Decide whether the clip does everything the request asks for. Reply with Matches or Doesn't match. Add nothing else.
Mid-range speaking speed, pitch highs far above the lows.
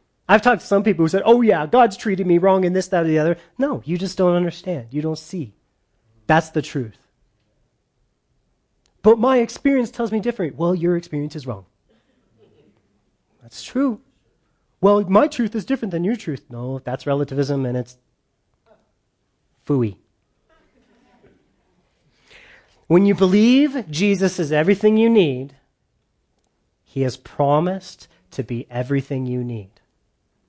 Matches